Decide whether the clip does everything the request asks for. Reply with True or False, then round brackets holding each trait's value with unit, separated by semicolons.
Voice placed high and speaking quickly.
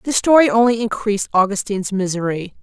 False (210 Hz; 135 wpm)